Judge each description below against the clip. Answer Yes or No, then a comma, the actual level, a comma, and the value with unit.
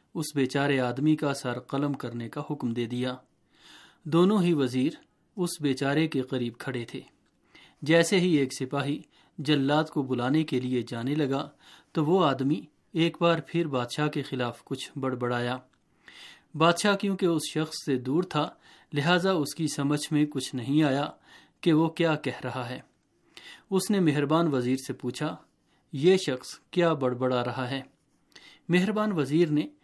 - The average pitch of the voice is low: No, medium, 145 Hz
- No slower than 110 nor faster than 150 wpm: No, average, 160 wpm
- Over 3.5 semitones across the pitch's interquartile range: Yes, average, 3.9 semitones